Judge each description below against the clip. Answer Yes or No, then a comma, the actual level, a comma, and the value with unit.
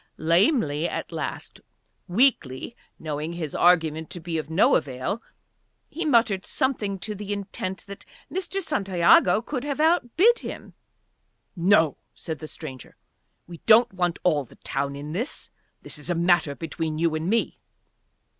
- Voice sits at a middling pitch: Yes, medium, 175 Hz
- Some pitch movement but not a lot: No, wide, 6.1 semitones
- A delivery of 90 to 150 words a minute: Yes, average, 145 wpm